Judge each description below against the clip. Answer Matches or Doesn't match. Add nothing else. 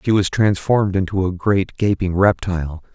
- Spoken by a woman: Doesn't match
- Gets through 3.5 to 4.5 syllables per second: Doesn't match